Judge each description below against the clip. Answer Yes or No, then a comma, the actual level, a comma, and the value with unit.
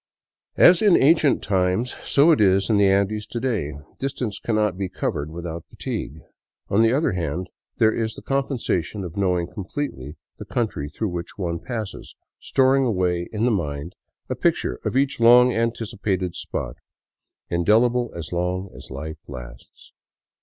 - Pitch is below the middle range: Yes, low, 100 Hz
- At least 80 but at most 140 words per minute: No, average, 160 wpm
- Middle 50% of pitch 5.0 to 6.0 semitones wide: Yes, wide, 5.5 semitones